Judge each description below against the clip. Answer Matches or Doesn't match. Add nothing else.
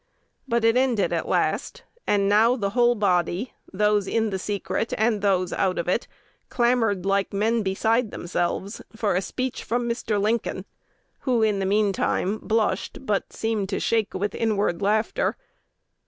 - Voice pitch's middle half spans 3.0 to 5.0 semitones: Doesn't match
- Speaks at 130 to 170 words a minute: Matches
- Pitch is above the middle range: Matches